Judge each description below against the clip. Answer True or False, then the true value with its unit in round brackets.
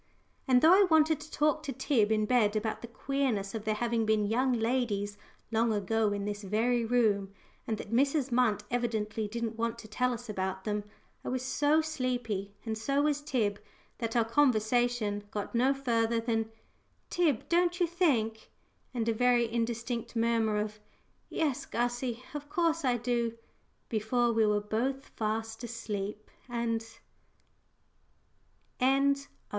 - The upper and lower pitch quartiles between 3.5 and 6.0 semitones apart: False (3.1 semitones)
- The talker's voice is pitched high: True (235 Hz)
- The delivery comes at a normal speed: True (160 wpm)